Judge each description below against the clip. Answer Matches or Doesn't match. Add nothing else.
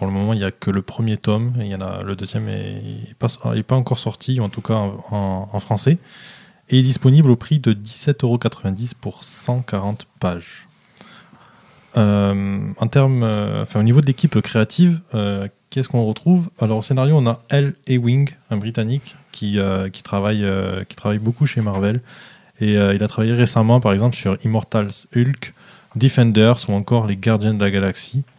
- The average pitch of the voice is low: Matches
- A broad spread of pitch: Doesn't match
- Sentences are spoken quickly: Doesn't match